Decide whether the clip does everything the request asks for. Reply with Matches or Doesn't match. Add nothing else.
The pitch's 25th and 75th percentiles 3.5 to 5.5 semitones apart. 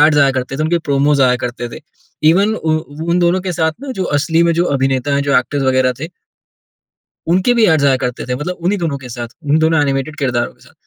Matches